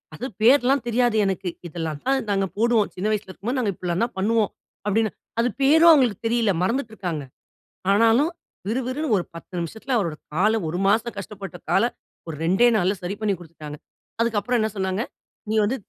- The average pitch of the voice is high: Yes, high, 215 Hz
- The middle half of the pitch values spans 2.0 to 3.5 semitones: No, average, 4.3 semitones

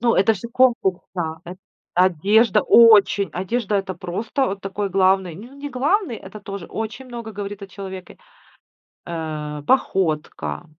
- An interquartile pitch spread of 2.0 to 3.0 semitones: No, average, 3.9 semitones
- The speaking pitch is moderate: No, high, 200 Hz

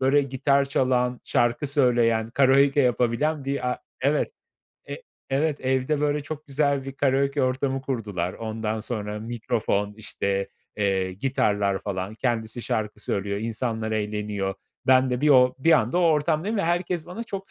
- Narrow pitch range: No, average, 4.3 semitones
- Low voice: Yes, low, 125 Hz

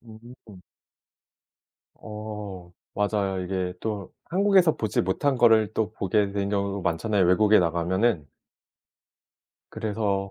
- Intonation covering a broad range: No, average, 2.7 semitones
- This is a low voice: Yes, low, 105 Hz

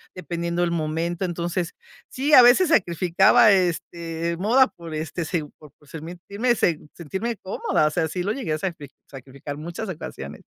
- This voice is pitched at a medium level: Yes, medium, 170 Hz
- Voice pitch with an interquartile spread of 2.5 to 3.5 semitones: Yes, average, 3.2 semitones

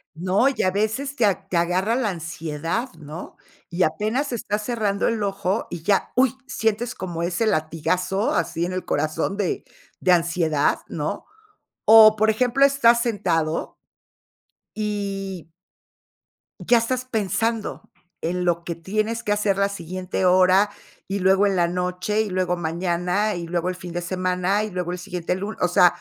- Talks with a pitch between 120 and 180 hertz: No, high, 190 Hz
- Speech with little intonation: No, average, 3.6 semitones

